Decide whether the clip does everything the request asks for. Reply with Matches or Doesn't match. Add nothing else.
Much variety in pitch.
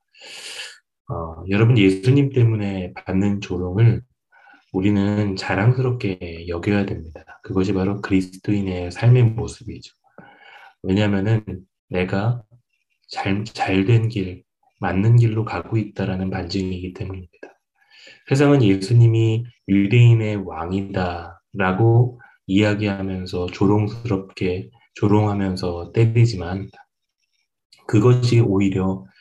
Doesn't match